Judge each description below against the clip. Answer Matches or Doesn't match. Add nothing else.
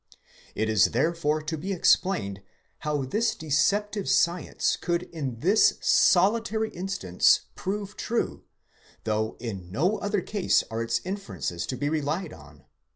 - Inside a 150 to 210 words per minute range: Doesn't match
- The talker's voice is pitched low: Doesn't match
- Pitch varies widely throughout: Matches